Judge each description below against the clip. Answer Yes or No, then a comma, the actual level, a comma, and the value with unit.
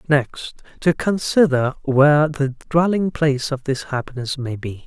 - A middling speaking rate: Yes, average, 150 wpm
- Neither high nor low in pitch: Yes, medium, 145 Hz